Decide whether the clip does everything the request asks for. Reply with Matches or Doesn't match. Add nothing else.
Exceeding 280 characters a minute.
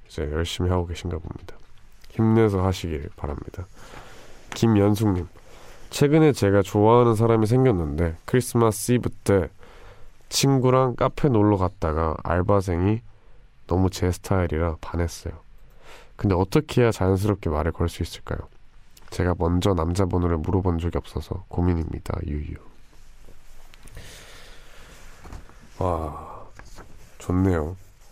Doesn't match